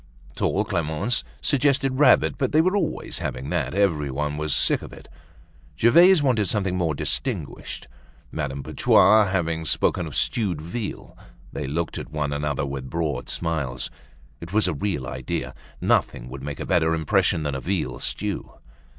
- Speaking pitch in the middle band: No, very low, 80 Hz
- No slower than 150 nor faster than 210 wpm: Yes, average, 160 wpm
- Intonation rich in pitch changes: Yes, wide, 6.4 semitones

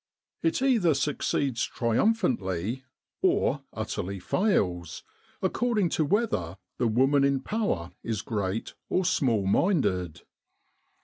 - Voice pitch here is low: Yes, low, 130 Hz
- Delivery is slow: Yes, slow, 105 wpm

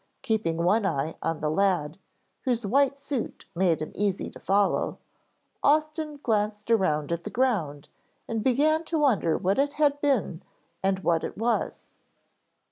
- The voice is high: Yes, high, 210 Hz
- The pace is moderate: Yes, average, 150 wpm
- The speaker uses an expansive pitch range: Yes, wide, 8.1 semitones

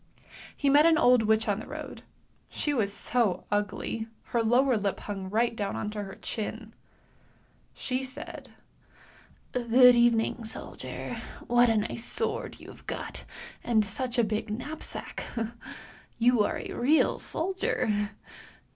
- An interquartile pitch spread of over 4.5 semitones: No, average, 3.0 semitones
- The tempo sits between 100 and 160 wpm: Yes, average, 140 wpm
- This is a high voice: Yes, high, 230 Hz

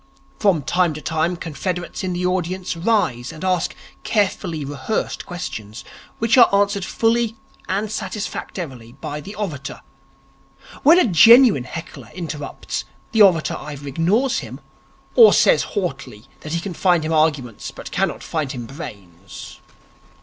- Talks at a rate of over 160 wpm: No, average, 140 wpm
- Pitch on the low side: No, medium, 175 Hz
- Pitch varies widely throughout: Yes, wide, 5.7 semitones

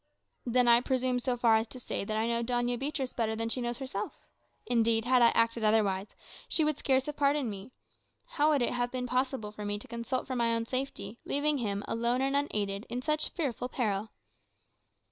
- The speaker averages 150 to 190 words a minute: No, fast, 205 wpm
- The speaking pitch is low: No, high, 240 Hz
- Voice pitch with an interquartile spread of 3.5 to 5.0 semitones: No, average, 2.8 semitones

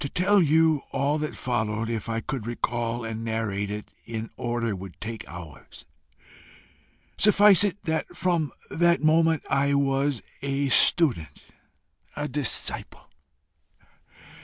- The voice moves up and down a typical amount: No, wide, 5.8 semitones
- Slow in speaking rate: Yes, slow, 125 wpm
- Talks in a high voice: No, low, 135 Hz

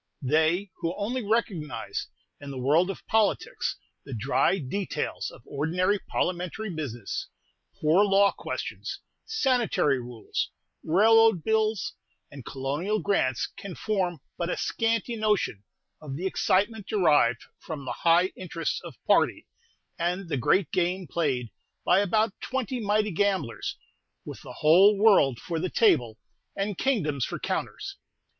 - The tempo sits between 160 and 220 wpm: No, slow, 135 wpm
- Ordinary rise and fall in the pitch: No, wide, 5.9 semitones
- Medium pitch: Yes, medium, 180 Hz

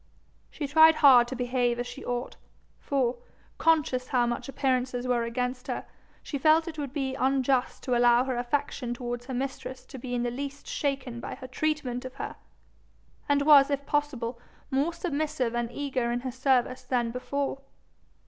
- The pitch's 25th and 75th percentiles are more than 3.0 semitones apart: No, narrow, 2.5 semitones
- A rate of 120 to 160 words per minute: No, average, 175 wpm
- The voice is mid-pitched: No, very high, 260 Hz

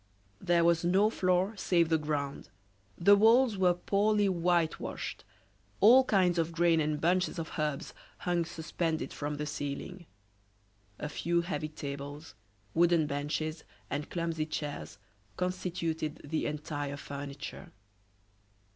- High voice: No, medium, 165 Hz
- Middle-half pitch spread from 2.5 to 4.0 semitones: Yes, average, 3.2 semitones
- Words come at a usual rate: No, slow, 120 wpm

